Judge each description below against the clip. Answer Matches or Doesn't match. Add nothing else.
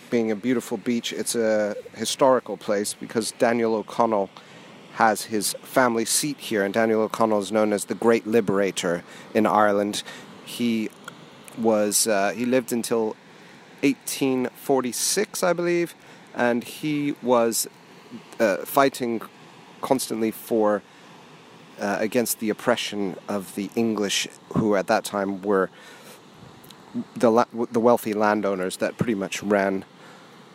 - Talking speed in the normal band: Doesn't match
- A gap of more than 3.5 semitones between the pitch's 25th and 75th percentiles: Doesn't match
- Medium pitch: Doesn't match